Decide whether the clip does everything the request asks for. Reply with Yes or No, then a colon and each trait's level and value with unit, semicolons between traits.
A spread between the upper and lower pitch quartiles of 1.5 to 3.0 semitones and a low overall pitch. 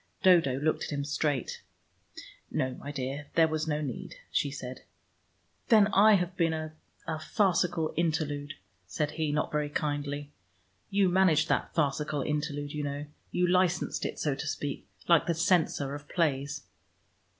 No: average, 2.7 semitones; medium, 150 Hz